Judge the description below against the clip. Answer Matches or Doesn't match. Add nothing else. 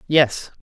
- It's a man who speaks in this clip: Matches